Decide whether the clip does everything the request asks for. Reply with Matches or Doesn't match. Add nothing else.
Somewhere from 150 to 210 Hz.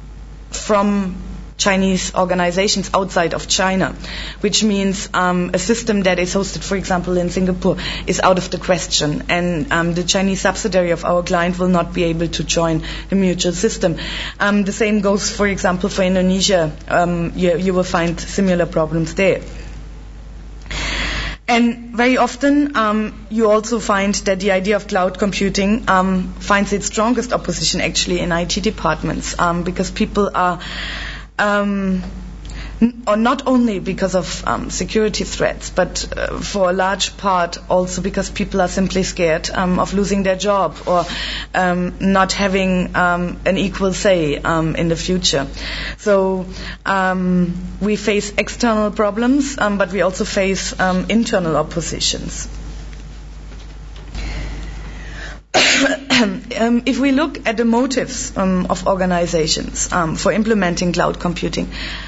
Matches